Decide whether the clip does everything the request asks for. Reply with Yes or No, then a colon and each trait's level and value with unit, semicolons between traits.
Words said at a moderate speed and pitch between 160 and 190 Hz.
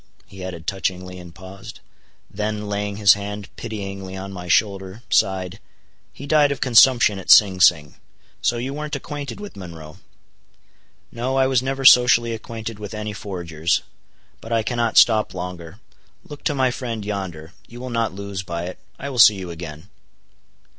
No: average, 165 wpm; low, 105 Hz